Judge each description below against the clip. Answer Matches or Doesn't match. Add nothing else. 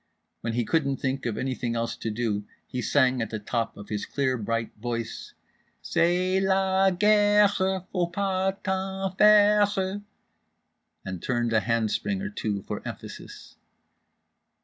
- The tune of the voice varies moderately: Doesn't match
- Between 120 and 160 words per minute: Matches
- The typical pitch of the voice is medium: Matches